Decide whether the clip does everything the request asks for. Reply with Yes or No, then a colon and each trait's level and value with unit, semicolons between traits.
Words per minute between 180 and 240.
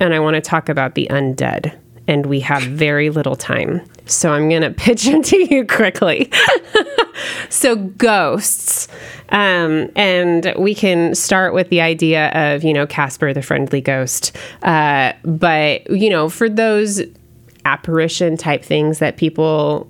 No: average, 150 wpm